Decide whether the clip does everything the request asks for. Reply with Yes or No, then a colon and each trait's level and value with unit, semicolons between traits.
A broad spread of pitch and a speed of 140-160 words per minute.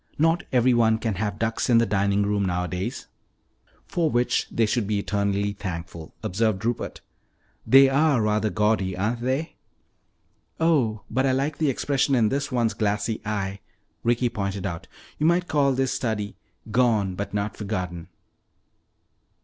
No: average, 4.1 semitones; average, 150 wpm